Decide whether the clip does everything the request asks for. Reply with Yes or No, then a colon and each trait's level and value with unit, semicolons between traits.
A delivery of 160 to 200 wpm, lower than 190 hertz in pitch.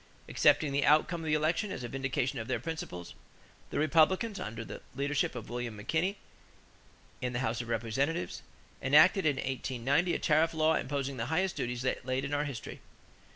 Yes: average, 180 wpm; medium, 140 Hz